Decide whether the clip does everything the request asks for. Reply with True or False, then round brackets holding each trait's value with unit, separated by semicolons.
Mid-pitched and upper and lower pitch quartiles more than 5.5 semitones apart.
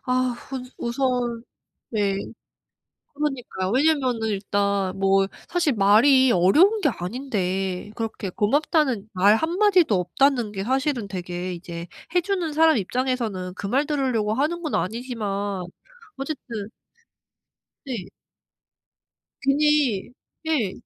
False (235 Hz; 6.2 semitones)